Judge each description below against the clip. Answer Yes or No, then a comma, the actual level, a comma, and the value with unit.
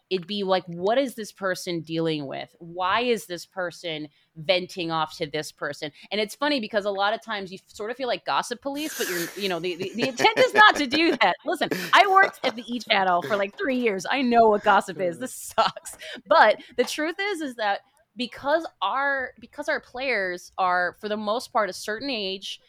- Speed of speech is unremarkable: No, fast, 220 wpm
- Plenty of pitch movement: Yes, wide, 6.3 semitones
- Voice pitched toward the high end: Yes, high, 205 Hz